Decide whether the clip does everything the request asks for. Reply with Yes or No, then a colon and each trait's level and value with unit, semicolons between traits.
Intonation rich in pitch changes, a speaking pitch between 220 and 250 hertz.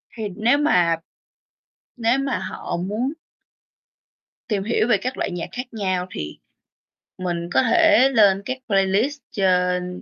No: wide, 5.7 semitones; high, 205 Hz